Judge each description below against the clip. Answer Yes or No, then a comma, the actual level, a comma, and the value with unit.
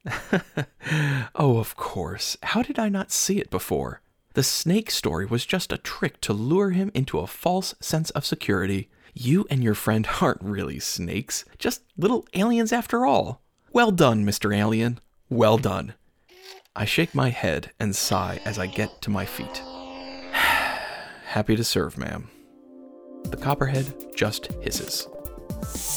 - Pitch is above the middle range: No, low, 125 Hz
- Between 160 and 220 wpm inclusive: No, average, 150 wpm